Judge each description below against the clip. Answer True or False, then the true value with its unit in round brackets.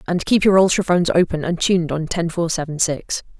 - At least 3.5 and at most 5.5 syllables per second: False (5.8 syllables/s)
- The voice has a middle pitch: True (170 Hz)